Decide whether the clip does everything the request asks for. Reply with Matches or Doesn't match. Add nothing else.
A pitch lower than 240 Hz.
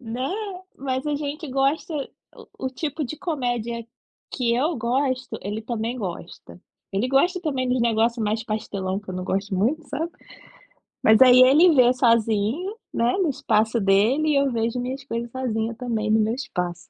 Doesn't match